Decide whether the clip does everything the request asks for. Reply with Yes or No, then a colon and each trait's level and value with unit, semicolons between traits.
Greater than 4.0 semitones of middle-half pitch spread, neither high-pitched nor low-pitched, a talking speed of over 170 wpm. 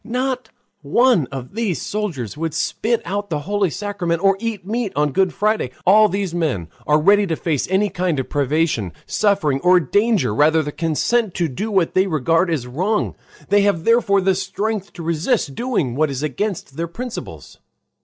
Yes: average, 5.2 semitones; medium, 180 Hz; average, 180 wpm